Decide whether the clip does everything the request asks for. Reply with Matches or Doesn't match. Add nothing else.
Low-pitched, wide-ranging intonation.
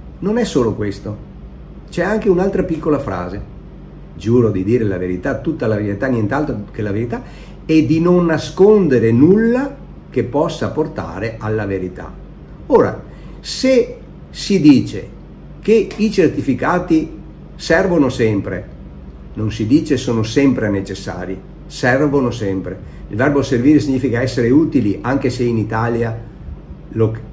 Matches